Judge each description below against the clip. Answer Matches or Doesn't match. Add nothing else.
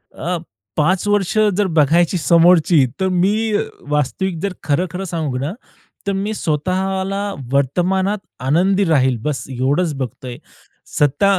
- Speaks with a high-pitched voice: Doesn't match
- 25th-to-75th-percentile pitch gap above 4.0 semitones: Matches